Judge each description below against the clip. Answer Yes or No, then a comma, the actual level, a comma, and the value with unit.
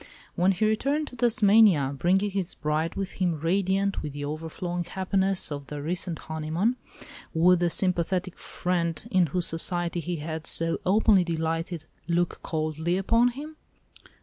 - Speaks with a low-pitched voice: No, medium, 175 Hz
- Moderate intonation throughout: Yes, average, 3.3 semitones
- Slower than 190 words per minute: Yes, average, 150 wpm